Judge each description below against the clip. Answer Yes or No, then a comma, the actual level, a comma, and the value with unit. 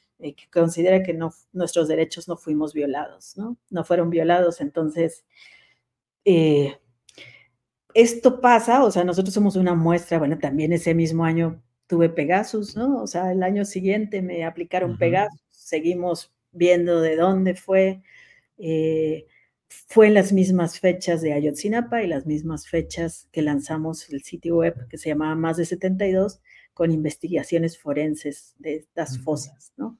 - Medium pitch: Yes, medium, 170 Hz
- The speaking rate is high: No, average, 150 wpm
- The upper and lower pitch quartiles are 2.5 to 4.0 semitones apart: Yes, average, 3.0 semitones